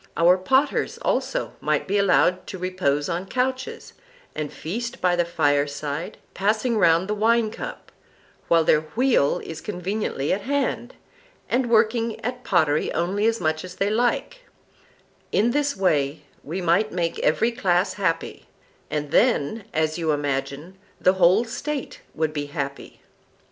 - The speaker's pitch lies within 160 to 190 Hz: Yes, medium, 185 Hz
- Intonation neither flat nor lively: No, wide, 6.4 semitones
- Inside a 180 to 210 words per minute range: No, average, 140 wpm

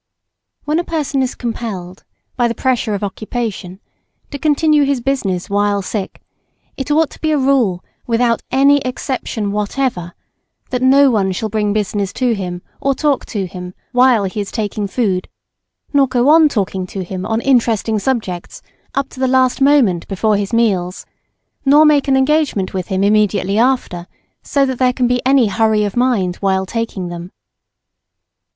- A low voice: No, high, 230 Hz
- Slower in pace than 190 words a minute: Yes, average, 165 wpm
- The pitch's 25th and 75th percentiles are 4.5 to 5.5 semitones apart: Yes, average, 5.2 semitones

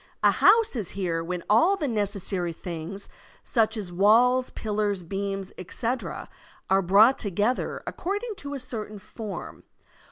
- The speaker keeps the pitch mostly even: No, average, 4.3 semitones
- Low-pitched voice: No, high, 210 Hz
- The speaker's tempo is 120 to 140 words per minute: Yes, slow, 135 wpm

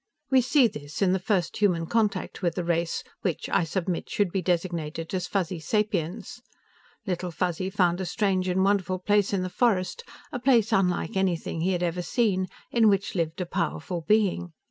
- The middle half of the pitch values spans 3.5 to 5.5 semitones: No, average, 2.9 semitones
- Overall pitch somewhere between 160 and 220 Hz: Yes, medium, 185 Hz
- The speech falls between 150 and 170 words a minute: No, average, 185 wpm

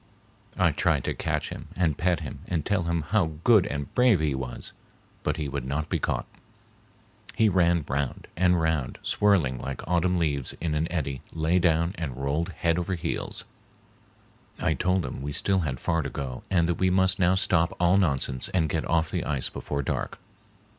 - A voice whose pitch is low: Yes, very low, 85 Hz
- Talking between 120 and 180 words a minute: No, average, 190 wpm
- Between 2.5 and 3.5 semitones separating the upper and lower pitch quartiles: No, average, 4.1 semitones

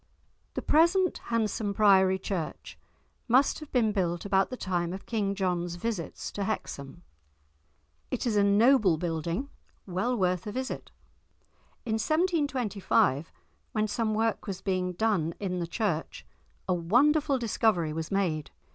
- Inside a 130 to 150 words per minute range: Yes, average, 140 wpm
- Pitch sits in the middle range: No, high, 200 Hz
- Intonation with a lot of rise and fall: No, average, 4.6 semitones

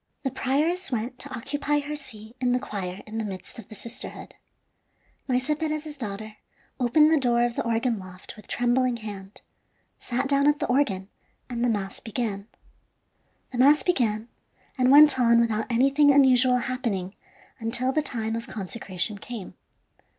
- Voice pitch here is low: No, high, 240 Hz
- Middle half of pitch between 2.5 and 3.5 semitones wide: No, average, 4.0 semitones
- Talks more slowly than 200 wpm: Yes, average, 160 wpm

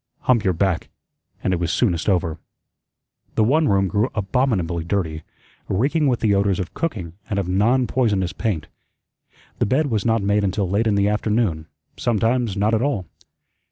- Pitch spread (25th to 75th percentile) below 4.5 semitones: Yes, average, 3.9 semitones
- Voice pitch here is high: No, low, 100 Hz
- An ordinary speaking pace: Yes, average, 170 wpm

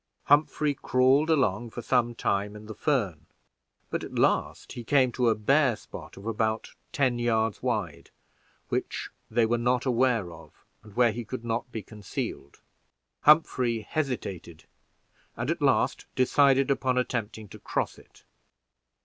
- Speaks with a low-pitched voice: Yes, low, 120 Hz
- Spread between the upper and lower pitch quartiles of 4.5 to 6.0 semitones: No, average, 3.3 semitones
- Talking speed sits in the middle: Yes, average, 150 wpm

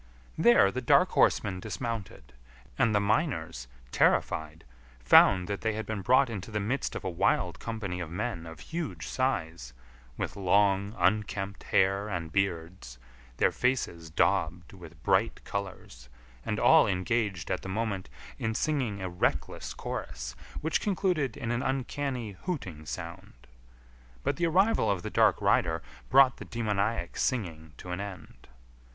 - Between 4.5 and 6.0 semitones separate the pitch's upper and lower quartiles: Yes, average, 5.2 semitones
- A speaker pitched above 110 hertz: No, low, 100 Hz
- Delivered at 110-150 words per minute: Yes, average, 145 wpm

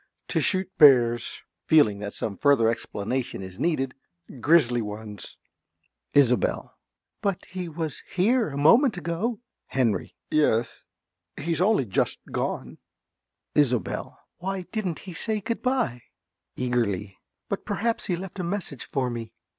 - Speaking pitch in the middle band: Yes, medium, 145 Hz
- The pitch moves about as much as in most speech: No, wide, 7.9 semitones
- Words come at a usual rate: No, slow, 130 wpm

